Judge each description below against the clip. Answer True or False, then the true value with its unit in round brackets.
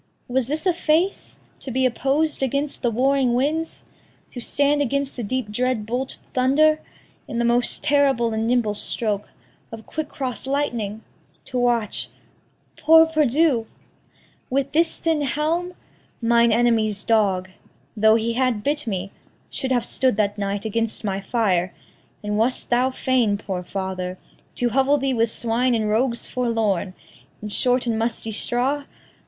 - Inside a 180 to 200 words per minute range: False (150 wpm)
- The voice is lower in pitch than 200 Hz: False (245 Hz)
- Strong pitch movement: False (3.9 semitones)